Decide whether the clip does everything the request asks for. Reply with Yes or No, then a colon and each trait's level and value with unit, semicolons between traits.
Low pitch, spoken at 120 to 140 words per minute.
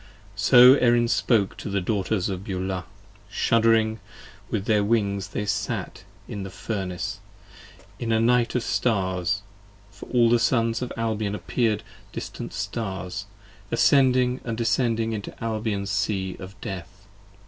Yes: low, 110 Hz; slow, 135 wpm